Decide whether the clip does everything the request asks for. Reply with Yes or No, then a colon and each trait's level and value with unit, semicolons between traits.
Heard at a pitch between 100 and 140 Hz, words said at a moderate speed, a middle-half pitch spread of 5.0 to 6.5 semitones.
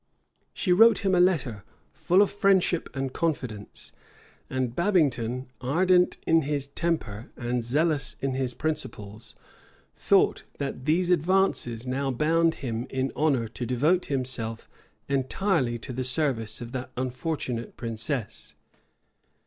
No: low, 135 Hz; slow, 125 wpm; average, 5.3 semitones